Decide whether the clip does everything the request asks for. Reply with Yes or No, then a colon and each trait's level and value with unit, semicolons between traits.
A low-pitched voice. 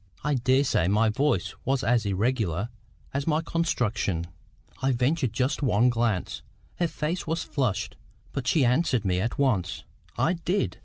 Yes: low, 125 Hz